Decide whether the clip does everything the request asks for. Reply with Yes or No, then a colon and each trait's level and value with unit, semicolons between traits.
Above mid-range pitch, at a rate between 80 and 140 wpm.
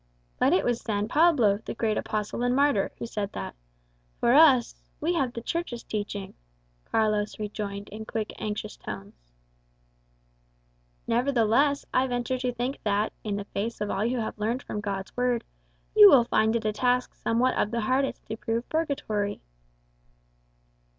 No: high, 225 Hz; average, 165 wpm